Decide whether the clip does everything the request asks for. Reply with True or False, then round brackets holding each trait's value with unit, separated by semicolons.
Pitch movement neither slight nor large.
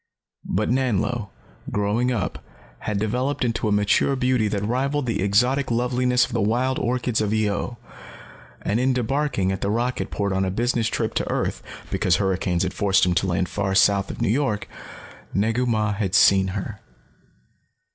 True (3.8 semitones)